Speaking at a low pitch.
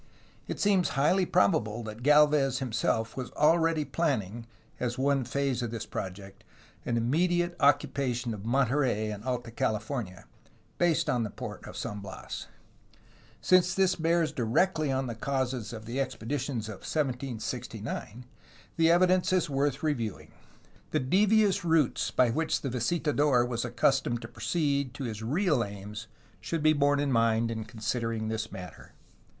Yes: low, 130 Hz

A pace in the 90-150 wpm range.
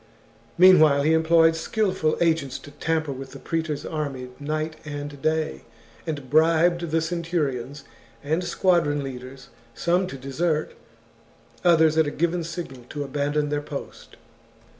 Yes: average, 145 wpm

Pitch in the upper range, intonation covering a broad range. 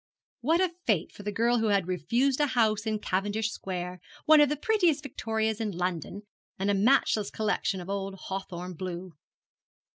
No: high, 210 Hz; average, 4.2 semitones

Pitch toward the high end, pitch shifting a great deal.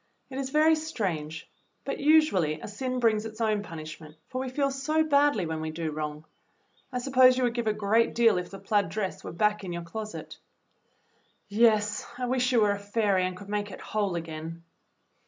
Yes: high, 210 Hz; wide, 6.3 semitones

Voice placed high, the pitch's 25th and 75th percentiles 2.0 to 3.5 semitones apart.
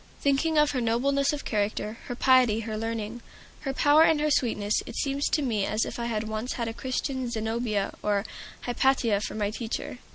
No: high, 235 Hz; average, 3.9 semitones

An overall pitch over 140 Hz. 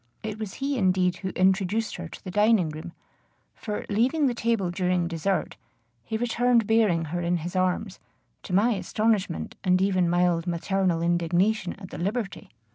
Yes: high, 190 Hz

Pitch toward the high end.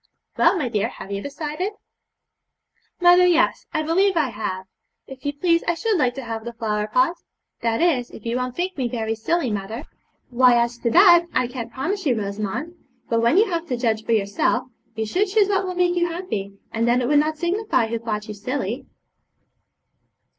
Yes: very high, 255 Hz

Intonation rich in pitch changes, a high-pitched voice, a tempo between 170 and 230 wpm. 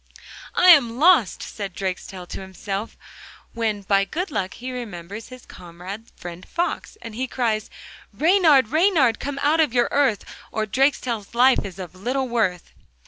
No: wide, 5.7 semitones; high, 230 Hz; average, 155 wpm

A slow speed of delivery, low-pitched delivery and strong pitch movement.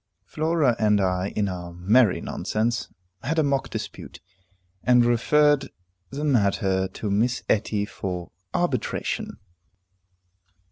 Yes: slow, 110 wpm; low, 110 Hz; wide, 5.7 semitones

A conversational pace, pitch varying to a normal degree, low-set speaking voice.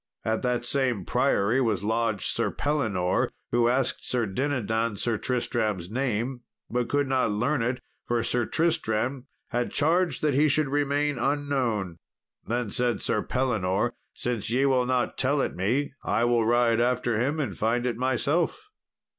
Yes: average, 155 wpm; average, 3.2 semitones; low, 120 Hz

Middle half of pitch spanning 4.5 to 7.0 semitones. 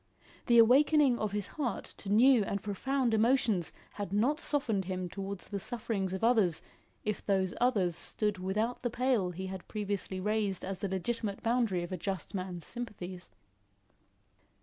No: average, 4.0 semitones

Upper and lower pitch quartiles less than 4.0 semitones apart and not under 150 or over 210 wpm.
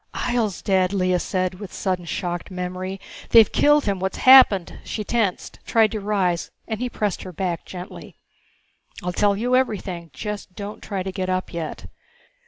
Yes: average, 2.7 semitones; average, 170 wpm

